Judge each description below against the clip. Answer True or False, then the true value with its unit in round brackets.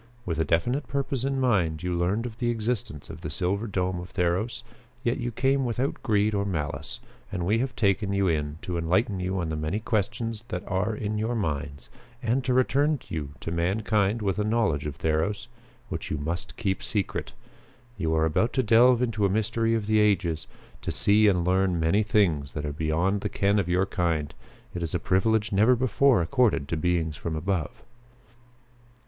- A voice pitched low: True (100 Hz)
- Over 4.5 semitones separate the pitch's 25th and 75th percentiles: True (5.1 semitones)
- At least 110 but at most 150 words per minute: False (195 wpm)